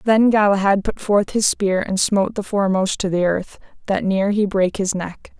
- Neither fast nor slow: No, fast, 210 wpm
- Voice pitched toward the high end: Yes, high, 200 Hz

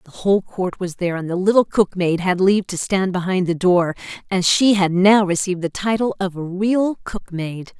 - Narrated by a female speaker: Yes, female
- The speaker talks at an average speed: No, fast, 225 wpm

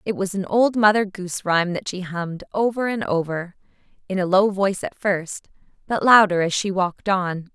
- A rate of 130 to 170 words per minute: No, average, 200 wpm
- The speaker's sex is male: No, female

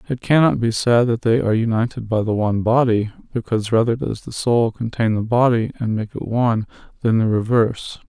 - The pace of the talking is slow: No, average, 200 wpm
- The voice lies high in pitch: No, low, 115 Hz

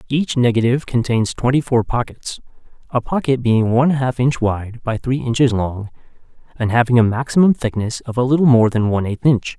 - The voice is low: Yes, low, 120 Hz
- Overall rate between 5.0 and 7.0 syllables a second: Yes, 5.5 syllables/s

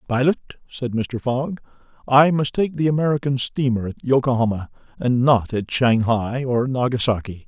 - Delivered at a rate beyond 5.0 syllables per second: No, 4.9 syllables/s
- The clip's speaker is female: No, male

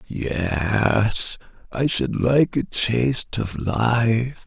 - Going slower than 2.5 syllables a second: Yes, 2.3 syllables/s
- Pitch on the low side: Yes, low, 110 Hz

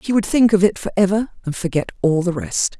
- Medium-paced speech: No, fast, 260 wpm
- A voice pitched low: No, medium, 185 Hz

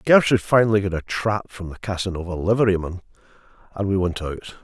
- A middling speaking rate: Yes, average, 170 wpm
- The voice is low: Yes, low, 100 Hz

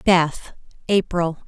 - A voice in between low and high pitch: Yes, medium, 175 Hz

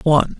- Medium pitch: Yes, medium, 155 Hz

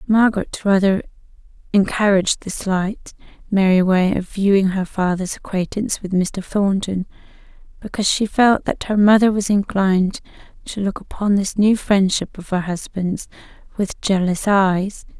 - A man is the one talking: No, female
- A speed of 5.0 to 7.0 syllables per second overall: No, 4.7 syllables/s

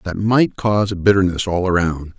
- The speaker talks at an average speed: Yes, average, 190 wpm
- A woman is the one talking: No, male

